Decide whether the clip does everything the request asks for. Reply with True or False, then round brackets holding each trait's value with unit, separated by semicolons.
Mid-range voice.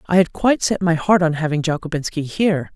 True (170 Hz)